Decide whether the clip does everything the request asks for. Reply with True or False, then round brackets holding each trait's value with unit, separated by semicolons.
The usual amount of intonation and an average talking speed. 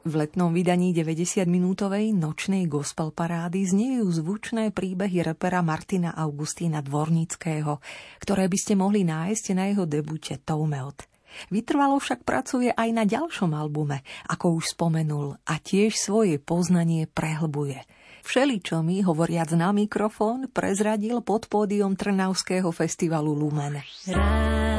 True (4.4 semitones; 120 wpm)